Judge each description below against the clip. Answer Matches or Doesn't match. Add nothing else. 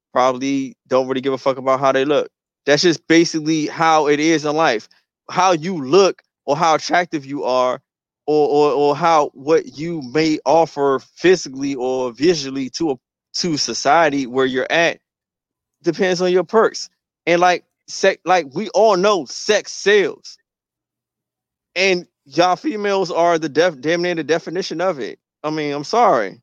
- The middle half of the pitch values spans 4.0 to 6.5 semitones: Matches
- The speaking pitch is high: Doesn't match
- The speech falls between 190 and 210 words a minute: Doesn't match